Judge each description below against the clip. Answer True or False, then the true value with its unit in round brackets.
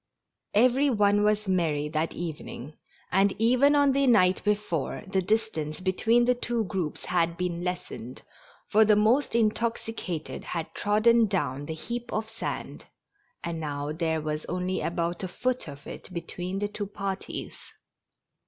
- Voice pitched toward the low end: False (190 Hz)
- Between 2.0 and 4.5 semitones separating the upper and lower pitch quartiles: False (5.0 semitones)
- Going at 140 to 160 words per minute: True (155 wpm)